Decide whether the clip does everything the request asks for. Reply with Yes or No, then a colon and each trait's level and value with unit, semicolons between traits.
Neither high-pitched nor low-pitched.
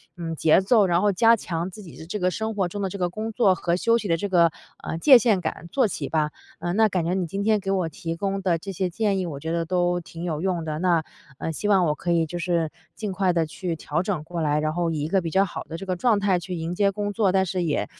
Yes: medium, 180 Hz